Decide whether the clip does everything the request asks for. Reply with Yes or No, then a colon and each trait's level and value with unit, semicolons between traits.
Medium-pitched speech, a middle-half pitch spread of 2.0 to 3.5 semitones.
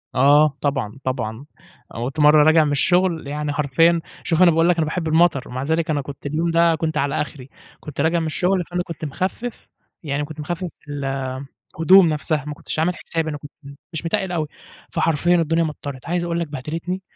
Yes: medium, 155 Hz; average, 2.8 semitones